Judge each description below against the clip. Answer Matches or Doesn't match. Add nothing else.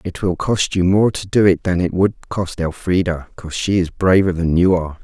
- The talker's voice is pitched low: Matches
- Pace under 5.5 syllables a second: Matches